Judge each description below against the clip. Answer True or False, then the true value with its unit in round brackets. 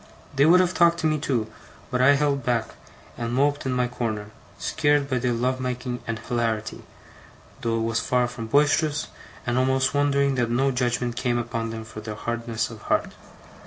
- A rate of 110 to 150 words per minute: False (190 wpm)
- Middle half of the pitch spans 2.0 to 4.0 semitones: True (3.1 semitones)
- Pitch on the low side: True (125 Hz)